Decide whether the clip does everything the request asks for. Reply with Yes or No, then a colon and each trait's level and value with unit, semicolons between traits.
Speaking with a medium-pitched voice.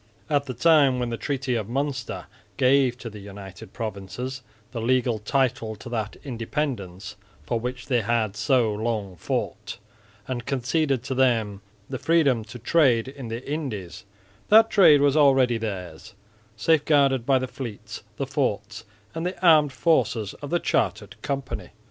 No: low, 125 Hz